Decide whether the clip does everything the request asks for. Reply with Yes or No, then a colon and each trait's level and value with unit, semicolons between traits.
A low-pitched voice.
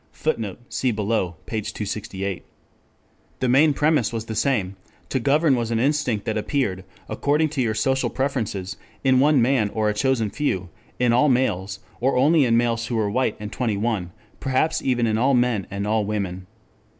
Yes: low, 115 Hz